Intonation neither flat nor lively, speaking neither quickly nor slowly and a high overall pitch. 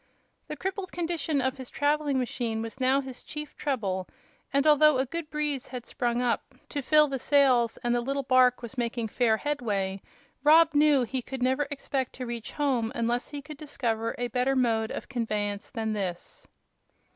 Yes: average, 3.6 semitones; average, 180 wpm; very high, 255 Hz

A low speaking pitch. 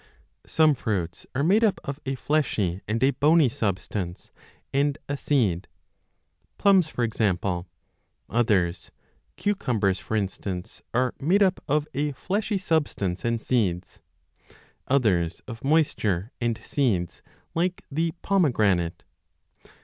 Yes: low, 120 Hz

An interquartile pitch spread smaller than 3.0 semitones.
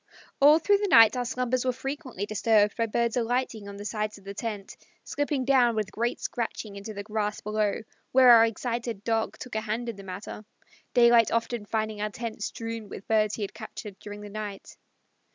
Yes: narrow, 2.4 semitones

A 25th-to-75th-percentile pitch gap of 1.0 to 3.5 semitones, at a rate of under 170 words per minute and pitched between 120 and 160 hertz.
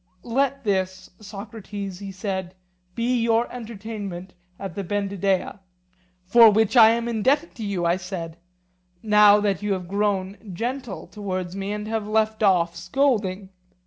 No: average, 2.8 semitones; average, 145 wpm; high, 205 Hz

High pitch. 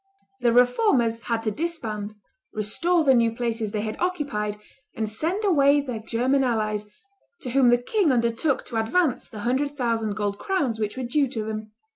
Yes: high, 240 Hz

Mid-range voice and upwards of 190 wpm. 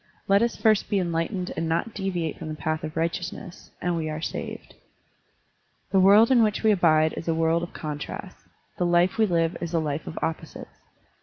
Yes: medium, 170 Hz; average, 200 wpm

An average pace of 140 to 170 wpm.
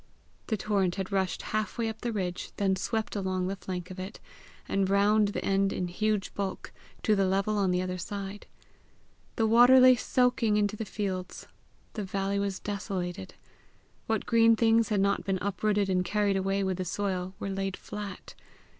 No: average, 180 wpm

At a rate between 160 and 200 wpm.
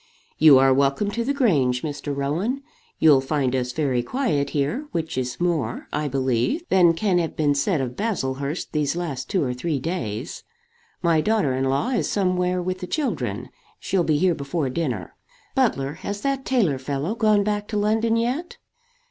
Yes: average, 175 wpm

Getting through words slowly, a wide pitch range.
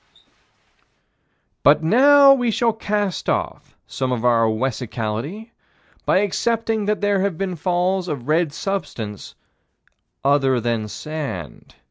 Yes: slow, 120 wpm; wide, 8.7 semitones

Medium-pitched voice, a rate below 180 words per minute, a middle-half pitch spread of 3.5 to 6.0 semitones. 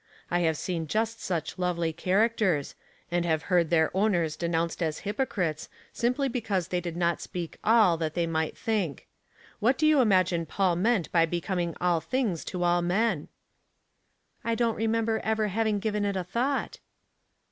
Yes: medium, 180 Hz; average, 170 wpm; average, 4.6 semitones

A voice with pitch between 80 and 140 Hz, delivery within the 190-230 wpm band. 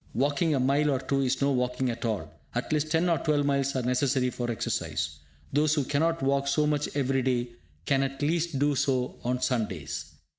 Yes: low, 135 Hz; average, 200 wpm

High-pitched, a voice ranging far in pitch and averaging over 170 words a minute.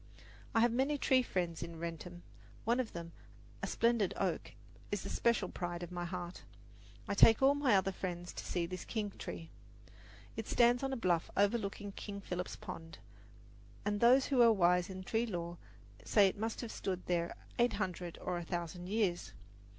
No: high, 195 Hz; average, 4.5 semitones; average, 180 wpm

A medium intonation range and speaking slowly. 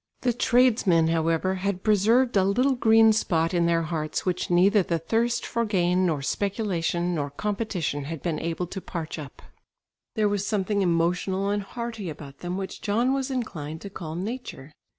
No: average, 4.7 semitones; average, 170 wpm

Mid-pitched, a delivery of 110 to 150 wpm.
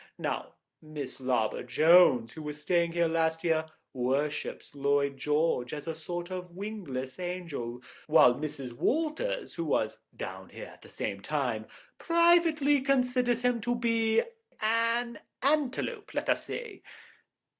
Yes: medium, 170 Hz; slow, 135 wpm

